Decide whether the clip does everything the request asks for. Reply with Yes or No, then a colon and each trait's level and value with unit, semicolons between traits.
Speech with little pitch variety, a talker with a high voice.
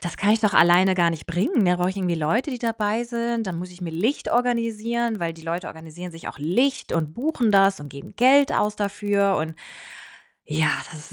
No: wide, 5.5 semitones; high, 195 Hz